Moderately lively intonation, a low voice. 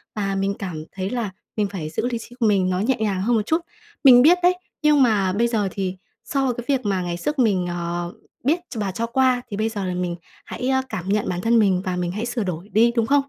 No: average, 4.6 semitones; high, 210 Hz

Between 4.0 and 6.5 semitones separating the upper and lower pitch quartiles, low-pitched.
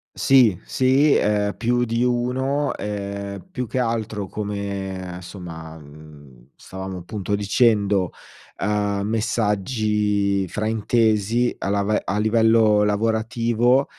No: average, 2.7 semitones; low, 105 Hz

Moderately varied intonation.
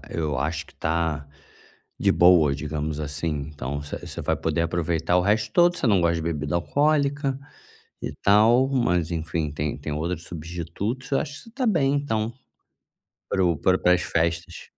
No: wide, 6.0 semitones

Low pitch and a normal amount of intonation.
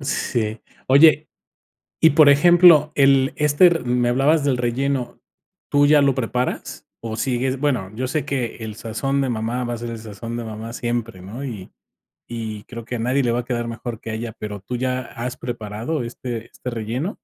Yes: low, 125 Hz; average, 3.2 semitones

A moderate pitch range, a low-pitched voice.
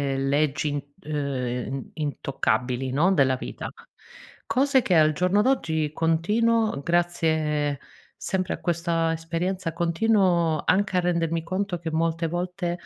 No: average, 3.3 semitones; medium, 165 Hz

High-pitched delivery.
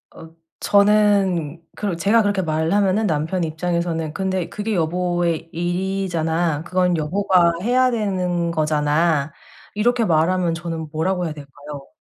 No: medium, 175 Hz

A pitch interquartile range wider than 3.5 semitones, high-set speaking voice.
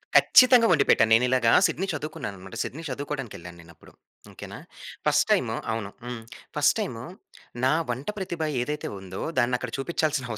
No: average, 5.2 semitones; low, 130 Hz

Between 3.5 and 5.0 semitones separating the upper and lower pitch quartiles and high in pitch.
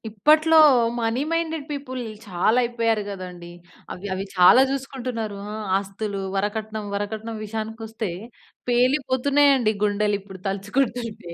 Yes: average, 4.0 semitones; high, 220 Hz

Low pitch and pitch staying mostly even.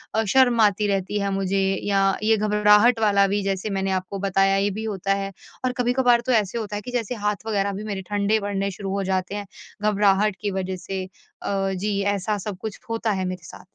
No: high, 205 Hz; narrow, 1.6 semitones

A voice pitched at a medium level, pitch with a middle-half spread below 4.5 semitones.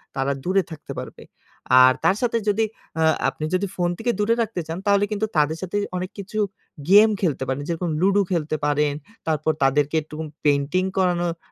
No: medium, 175 Hz; average, 5.0 semitones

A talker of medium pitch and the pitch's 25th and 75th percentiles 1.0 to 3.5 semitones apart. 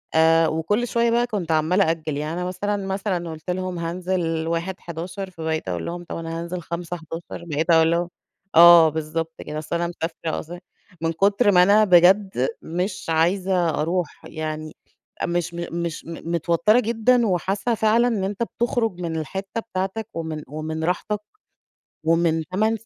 Yes: medium, 170 Hz; average, 3.0 semitones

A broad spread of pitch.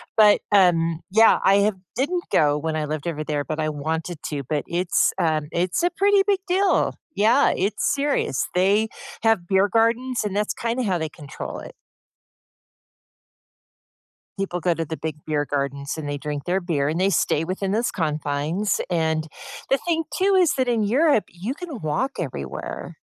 Yes: wide, 6.7 semitones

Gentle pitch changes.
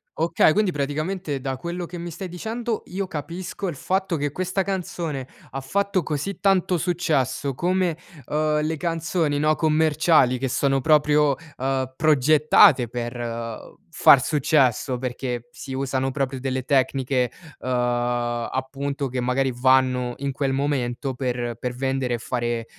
No: average, 4.3 semitones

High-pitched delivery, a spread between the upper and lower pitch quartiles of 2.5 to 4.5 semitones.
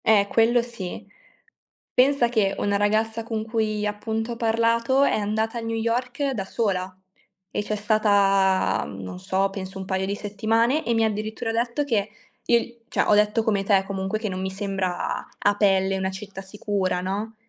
Yes: high, 210 Hz; average, 2.8 semitones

